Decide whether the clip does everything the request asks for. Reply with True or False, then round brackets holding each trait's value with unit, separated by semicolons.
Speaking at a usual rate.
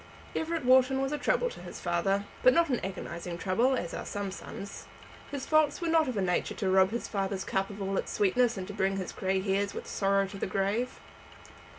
False (225 wpm)